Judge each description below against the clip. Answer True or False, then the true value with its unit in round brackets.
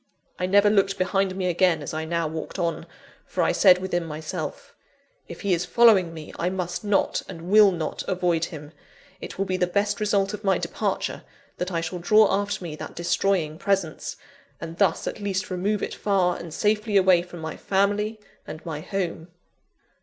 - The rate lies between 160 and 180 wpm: False (190 wpm)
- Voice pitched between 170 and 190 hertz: True (185 Hz)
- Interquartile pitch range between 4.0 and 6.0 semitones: False (3.0 semitones)